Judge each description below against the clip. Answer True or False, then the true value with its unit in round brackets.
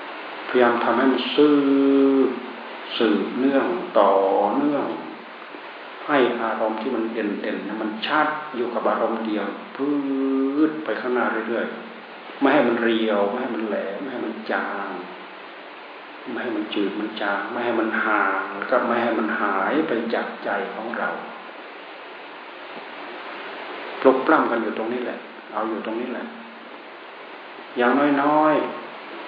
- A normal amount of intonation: True (3.8 semitones)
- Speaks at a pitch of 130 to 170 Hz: False (120 Hz)